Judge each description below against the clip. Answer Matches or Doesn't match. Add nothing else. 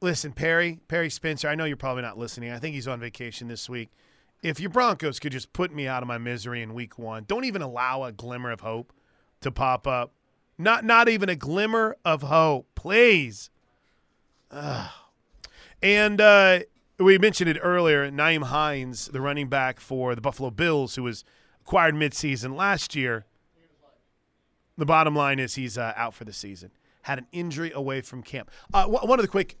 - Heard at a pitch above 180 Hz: Doesn't match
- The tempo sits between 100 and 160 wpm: Doesn't match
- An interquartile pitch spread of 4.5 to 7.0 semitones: Matches